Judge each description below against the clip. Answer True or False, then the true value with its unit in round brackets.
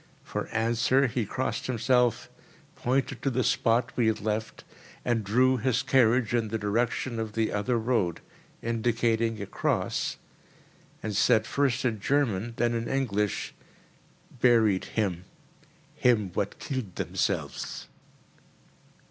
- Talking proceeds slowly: True (120 wpm)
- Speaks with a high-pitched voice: False (115 Hz)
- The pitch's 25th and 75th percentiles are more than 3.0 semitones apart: False (2.5 semitones)